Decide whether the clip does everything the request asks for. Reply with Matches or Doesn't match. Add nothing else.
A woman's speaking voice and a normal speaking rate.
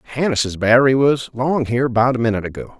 Doesn't match